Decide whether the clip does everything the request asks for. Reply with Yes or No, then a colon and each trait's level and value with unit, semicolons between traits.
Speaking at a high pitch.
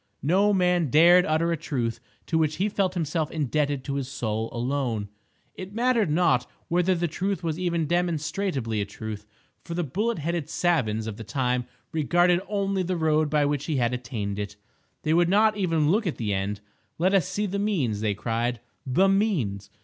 No: medium, 155 Hz